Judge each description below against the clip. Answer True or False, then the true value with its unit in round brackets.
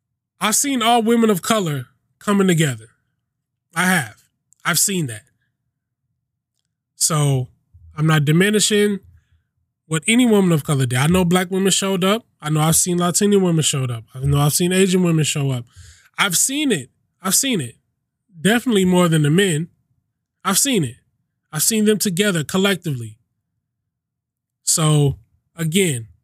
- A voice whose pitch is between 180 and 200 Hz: False (150 Hz)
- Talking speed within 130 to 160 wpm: True (150 wpm)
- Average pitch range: False (7.0 semitones)